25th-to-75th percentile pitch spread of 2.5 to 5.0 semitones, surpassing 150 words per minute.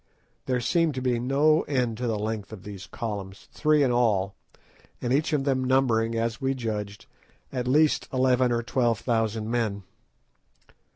Yes: average, 3.0 semitones; average, 160 wpm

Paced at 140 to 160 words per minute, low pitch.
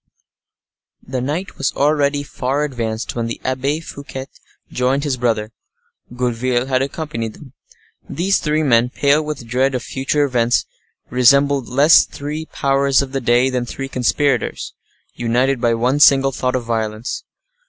Yes: average, 145 wpm; low, 130 Hz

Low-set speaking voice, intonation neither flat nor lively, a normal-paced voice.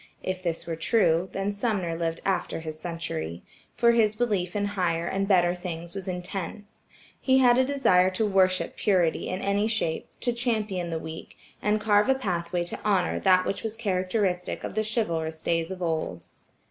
No: medium, 185 Hz; average, 3.7 semitones; average, 175 wpm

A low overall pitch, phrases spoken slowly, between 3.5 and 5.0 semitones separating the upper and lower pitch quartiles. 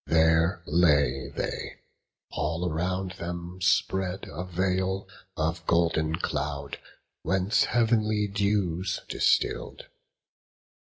No: very low, 90 Hz; slow, 90 wpm; average, 2.8 semitones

